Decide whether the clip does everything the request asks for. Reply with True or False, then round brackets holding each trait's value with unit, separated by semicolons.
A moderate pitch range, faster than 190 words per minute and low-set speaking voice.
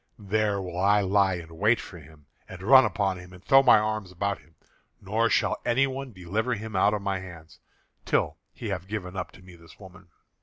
True (3.0 semitones; 205 wpm; 100 Hz)